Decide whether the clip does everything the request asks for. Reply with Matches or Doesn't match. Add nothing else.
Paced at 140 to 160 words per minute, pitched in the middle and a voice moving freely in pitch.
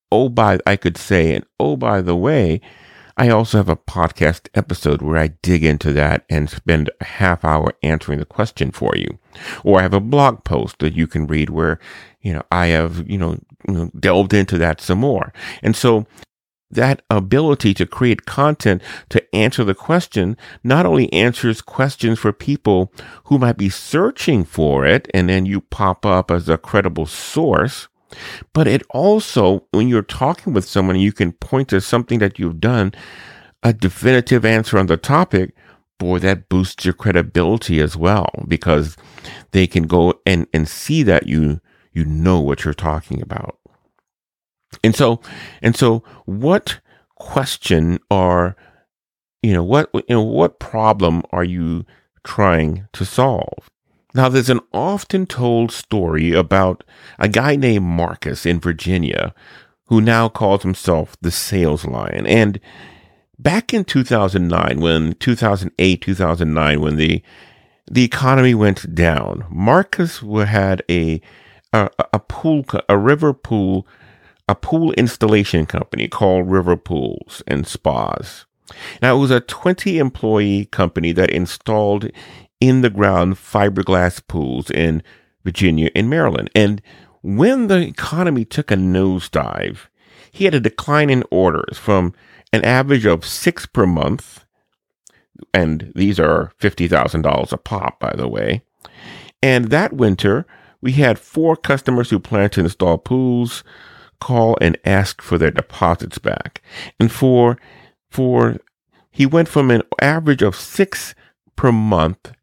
Doesn't match